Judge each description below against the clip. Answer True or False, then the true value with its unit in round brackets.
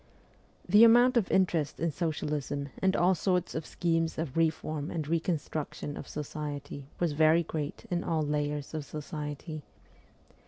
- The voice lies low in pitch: False (155 Hz)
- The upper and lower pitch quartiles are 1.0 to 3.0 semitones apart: True (2.6 semitones)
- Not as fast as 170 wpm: True (145 wpm)